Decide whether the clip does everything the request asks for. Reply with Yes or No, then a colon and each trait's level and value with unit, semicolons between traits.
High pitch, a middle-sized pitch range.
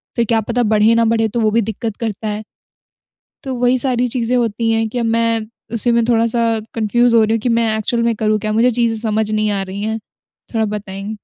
No: high, 225 Hz; narrow, 1.5 semitones